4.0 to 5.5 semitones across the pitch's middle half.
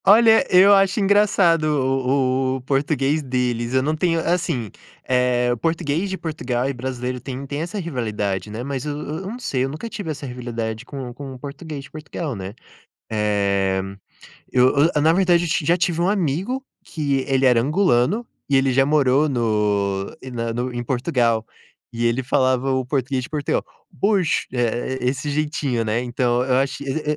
Yes: average, 4.4 semitones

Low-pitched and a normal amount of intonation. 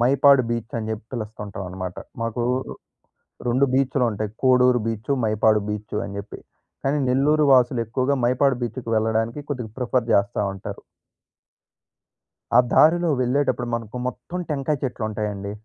Yes: low, 120 Hz; average, 3.5 semitones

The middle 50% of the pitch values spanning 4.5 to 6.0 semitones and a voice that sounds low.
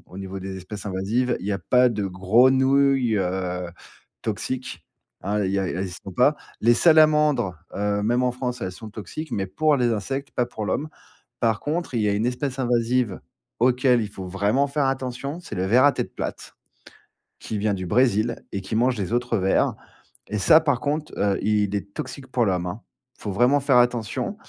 Yes: average, 4.8 semitones; low, 115 Hz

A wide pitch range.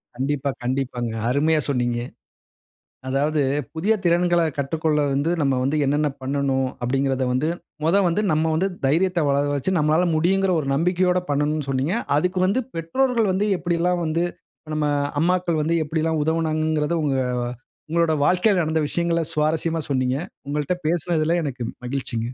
No: average, 3.6 semitones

